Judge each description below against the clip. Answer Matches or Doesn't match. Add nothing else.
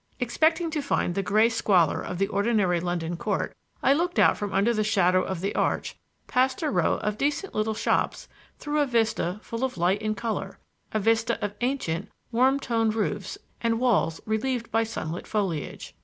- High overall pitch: Matches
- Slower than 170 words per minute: Doesn't match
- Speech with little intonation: Doesn't match